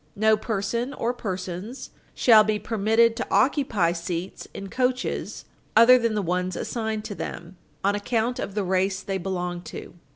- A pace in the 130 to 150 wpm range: No, average, 160 wpm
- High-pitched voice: Yes, high, 210 Hz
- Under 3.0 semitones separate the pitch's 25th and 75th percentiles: No, average, 3.7 semitones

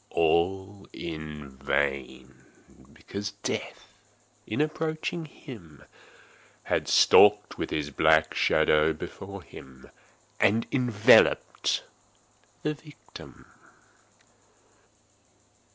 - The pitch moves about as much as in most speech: No, wide, 6.6 semitones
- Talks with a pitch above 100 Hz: No, very low, 85 Hz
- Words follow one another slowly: Yes, slow, 75 wpm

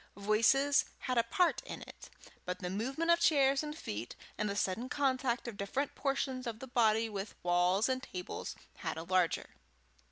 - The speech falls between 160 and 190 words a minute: Yes, average, 180 wpm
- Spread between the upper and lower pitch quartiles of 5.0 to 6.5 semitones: Yes, wide, 5.4 semitones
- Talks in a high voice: Yes, high, 235 Hz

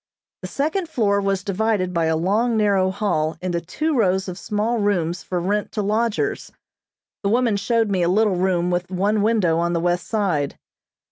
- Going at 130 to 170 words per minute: No, average, 185 wpm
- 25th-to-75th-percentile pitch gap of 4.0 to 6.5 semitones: No, average, 3.6 semitones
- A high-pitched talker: Yes, high, 195 Hz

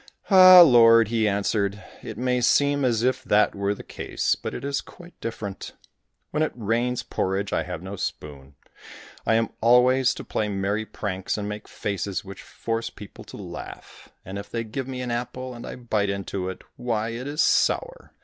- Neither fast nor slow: Yes, average, 190 wpm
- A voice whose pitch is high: No, low, 115 Hz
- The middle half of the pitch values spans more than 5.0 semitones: No, average, 3.9 semitones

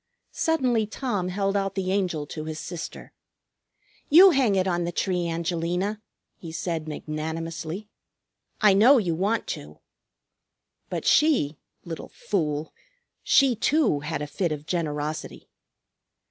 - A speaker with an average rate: No, slow, 130 wpm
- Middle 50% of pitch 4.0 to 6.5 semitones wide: Yes, average, 4.6 semitones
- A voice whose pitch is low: No, medium, 180 Hz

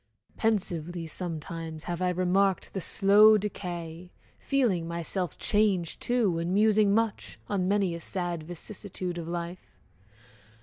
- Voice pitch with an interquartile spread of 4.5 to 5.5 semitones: No, average, 3.1 semitones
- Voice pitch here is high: No, medium, 180 Hz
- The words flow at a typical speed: No, slow, 125 wpm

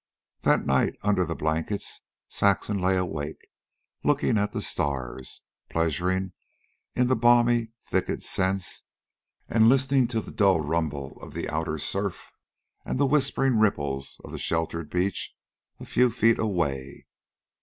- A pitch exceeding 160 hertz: No, very low, 95 Hz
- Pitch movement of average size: No, wide, 6.5 semitones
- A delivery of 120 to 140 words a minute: Yes, slow, 135 wpm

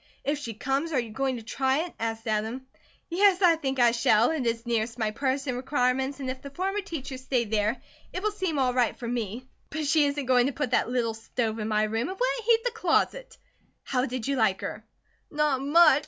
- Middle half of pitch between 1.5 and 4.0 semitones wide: No, average, 4.5 semitones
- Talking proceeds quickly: Yes, fast, 230 wpm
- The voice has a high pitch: Yes, very high, 260 Hz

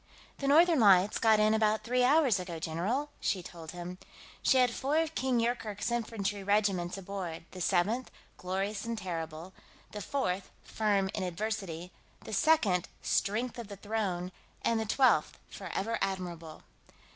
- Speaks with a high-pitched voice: Yes, high, 205 Hz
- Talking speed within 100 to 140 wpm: No, average, 150 wpm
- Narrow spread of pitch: No, average, 4.3 semitones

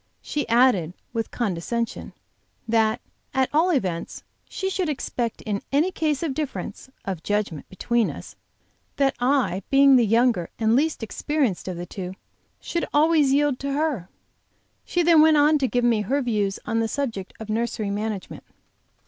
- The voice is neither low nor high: No, high, 240 Hz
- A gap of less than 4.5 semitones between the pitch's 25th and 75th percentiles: No, wide, 5.6 semitones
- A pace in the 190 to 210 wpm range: No, average, 160 wpm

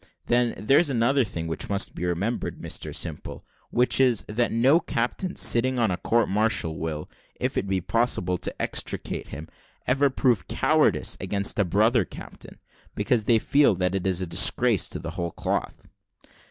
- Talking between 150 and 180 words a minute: Yes, average, 165 wpm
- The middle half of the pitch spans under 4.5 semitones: No, average, 5.2 semitones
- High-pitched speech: No, low, 110 Hz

